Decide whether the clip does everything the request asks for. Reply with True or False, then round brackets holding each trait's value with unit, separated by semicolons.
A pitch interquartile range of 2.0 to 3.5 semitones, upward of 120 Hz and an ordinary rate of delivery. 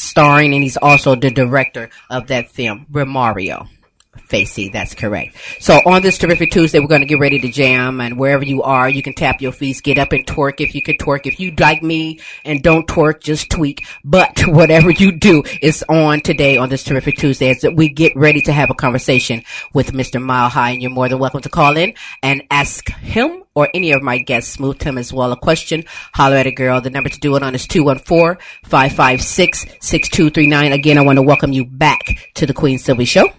False (3.0 semitones; 140 Hz; 215 wpm)